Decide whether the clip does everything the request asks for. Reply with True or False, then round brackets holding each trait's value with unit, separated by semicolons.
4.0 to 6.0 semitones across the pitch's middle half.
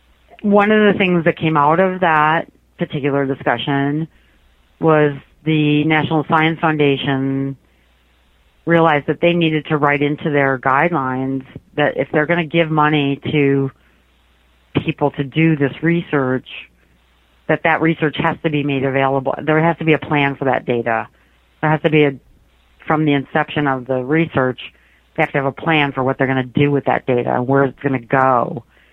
False (3.3 semitones)